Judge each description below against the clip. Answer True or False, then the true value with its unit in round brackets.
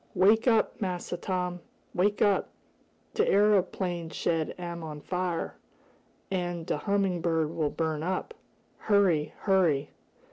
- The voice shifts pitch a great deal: False (3.0 semitones)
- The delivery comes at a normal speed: False (120 wpm)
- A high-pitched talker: False (180 Hz)